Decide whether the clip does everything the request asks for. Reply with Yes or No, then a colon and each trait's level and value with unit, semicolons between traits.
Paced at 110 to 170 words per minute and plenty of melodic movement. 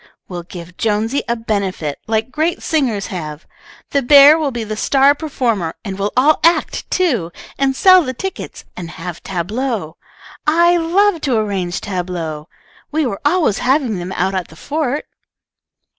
Yes: average, 160 wpm; wide, 8.1 semitones